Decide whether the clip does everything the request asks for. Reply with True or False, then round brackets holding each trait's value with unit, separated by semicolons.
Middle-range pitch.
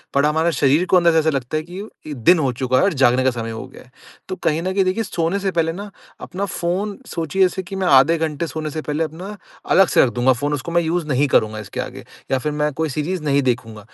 True (155 Hz)